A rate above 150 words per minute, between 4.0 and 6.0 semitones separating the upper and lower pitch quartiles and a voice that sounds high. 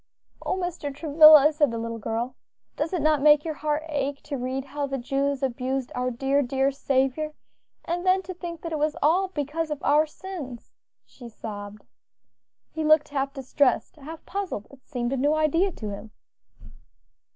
No: average, 175 wpm; average, 3.0 semitones; very high, 285 Hz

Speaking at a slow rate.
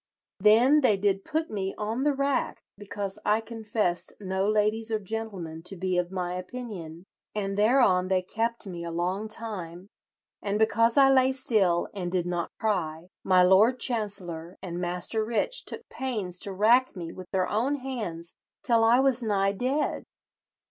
No: average, 165 wpm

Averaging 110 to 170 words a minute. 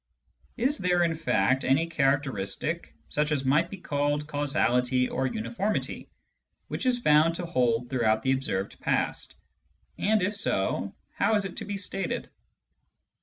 Yes: average, 145 wpm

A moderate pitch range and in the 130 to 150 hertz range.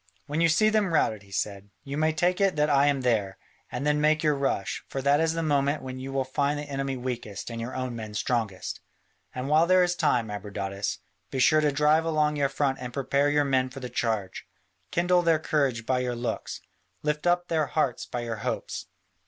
Yes: average, 4.0 semitones; medium, 140 Hz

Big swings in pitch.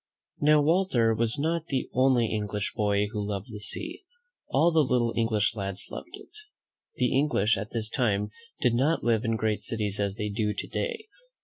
No: average, 5.0 semitones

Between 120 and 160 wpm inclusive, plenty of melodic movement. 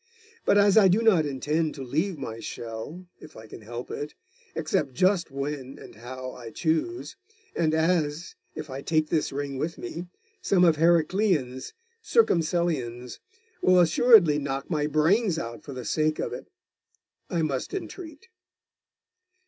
No: average, 150 wpm; average, 4.9 semitones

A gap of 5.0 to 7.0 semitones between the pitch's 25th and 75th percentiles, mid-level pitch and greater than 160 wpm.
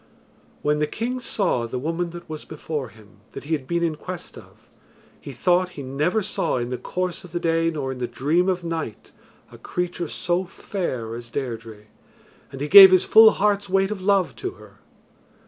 Yes: wide, 5.6 semitones; medium, 165 Hz; average, 200 wpm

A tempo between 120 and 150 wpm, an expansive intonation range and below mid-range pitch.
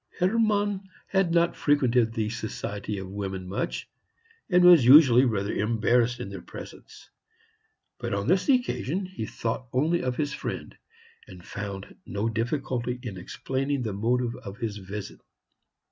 Yes: average, 145 wpm; wide, 6.7 semitones; low, 120 Hz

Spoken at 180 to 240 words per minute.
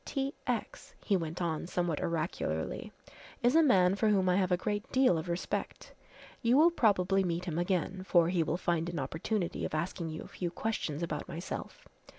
Yes: average, 190 wpm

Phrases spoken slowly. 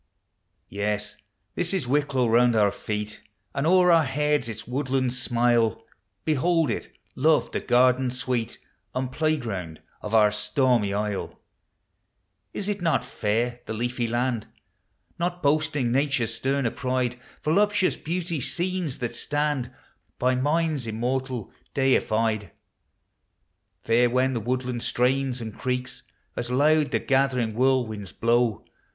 Yes: slow, 120 wpm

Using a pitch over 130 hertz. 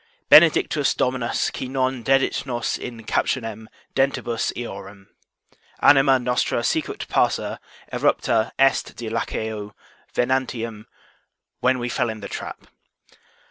No: low, 120 Hz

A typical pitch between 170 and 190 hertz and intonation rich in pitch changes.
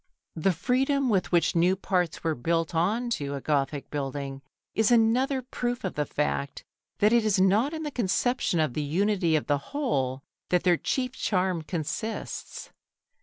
Yes: medium, 185 Hz; wide, 7.6 semitones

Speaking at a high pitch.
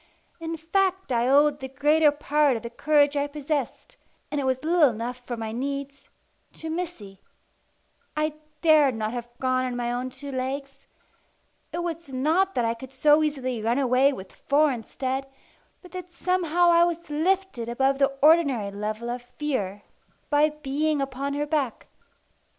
Yes: very high, 280 Hz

